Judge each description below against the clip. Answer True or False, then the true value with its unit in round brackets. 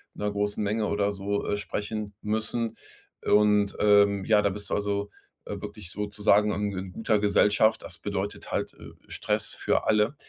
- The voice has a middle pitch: False (105 Hz)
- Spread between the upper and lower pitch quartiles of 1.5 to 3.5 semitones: False (0.7 semitones)